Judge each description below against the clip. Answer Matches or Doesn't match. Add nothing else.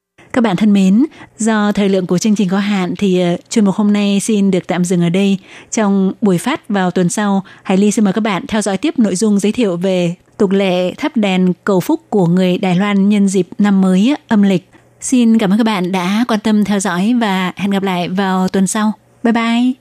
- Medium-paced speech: Matches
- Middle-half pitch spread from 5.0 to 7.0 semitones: Doesn't match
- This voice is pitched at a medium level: Doesn't match